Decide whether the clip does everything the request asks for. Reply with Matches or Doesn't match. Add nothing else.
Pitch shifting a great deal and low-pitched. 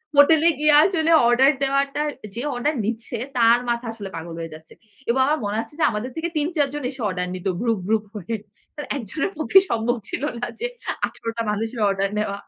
Doesn't match